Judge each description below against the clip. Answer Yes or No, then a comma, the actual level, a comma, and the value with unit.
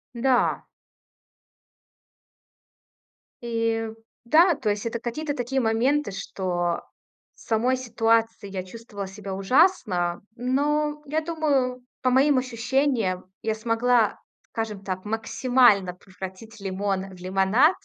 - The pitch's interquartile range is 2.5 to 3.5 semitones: No, average, 4.8 semitones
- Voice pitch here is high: Yes, high, 230 Hz